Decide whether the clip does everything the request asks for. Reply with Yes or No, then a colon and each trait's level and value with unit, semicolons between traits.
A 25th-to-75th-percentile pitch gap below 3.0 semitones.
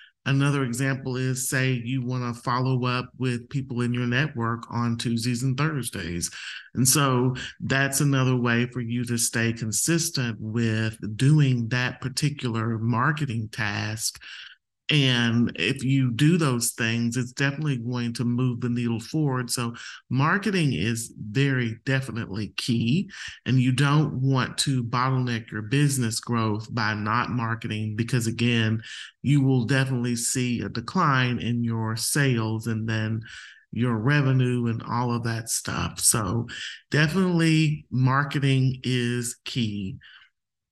Yes: narrow, 2.4 semitones